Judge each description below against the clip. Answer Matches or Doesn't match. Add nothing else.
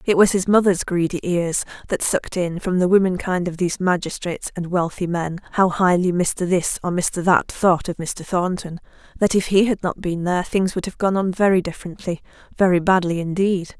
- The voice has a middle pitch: Matches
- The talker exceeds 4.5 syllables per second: Matches